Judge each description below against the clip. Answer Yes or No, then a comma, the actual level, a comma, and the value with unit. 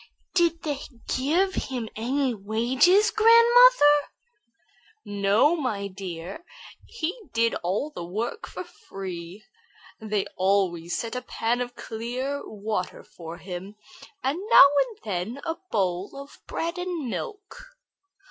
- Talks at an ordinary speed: No, slow, 120 wpm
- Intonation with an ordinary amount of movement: No, wide, 8.6 semitones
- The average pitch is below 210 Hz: No, high, 245 Hz